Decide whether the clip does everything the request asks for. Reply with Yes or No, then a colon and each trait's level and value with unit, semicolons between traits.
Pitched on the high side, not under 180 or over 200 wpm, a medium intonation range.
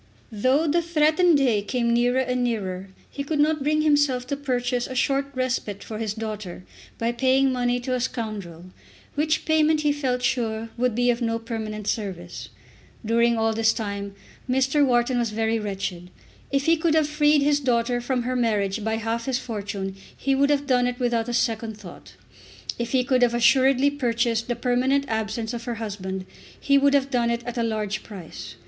Yes: high, 240 Hz; average, 190 wpm; average, 3.4 semitones